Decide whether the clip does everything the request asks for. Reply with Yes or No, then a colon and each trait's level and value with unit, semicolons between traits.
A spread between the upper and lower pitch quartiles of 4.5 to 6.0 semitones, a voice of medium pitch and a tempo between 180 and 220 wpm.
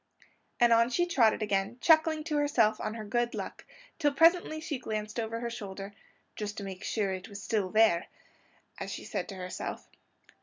No: wide, 5.6 semitones; high, 225 Hz; average, 190 wpm